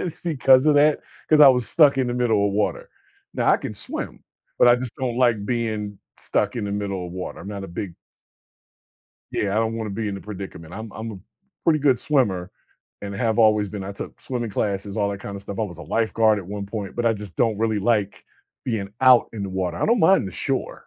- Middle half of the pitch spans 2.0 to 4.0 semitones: Yes, average, 3.5 semitones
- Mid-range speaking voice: No, low, 110 Hz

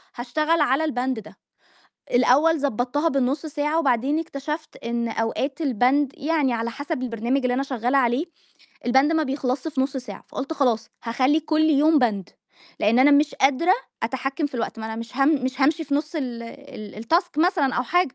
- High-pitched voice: Yes, very high, 270 Hz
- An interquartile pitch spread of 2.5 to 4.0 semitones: Yes, average, 3.7 semitones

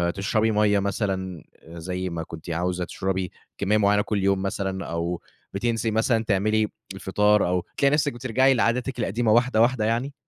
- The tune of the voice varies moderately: Yes, average, 3.4 semitones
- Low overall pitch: Yes, low, 105 Hz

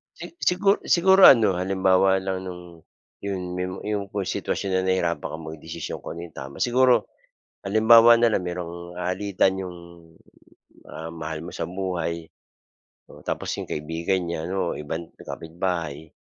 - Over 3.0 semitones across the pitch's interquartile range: No, average, 2.7 semitones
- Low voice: Yes, very low, 90 Hz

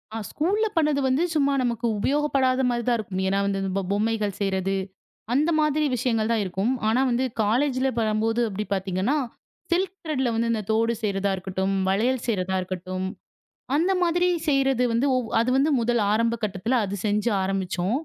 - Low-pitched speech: No, high, 230 Hz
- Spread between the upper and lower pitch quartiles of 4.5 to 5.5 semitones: Yes, average, 5.2 semitones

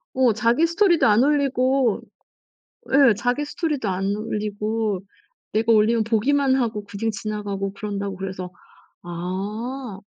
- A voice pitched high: Yes, high, 220 Hz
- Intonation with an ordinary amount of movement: Yes, average, 4.4 semitones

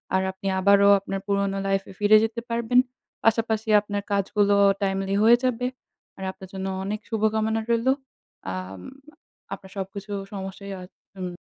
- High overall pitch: Yes, high, 200 Hz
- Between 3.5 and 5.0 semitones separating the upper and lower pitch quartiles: No, narrow, 2.4 semitones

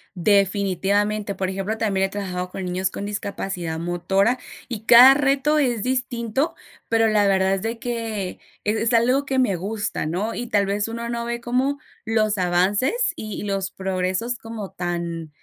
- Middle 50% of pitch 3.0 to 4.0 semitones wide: Yes, average, 3.6 semitones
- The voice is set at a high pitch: Yes, high, 205 Hz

